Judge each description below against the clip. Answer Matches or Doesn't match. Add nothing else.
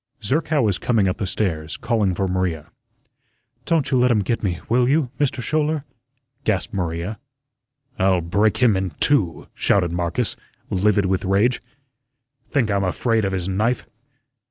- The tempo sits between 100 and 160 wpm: Matches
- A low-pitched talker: Matches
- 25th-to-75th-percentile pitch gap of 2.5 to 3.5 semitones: Doesn't match